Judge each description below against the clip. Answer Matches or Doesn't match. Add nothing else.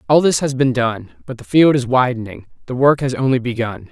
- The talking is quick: Matches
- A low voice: Matches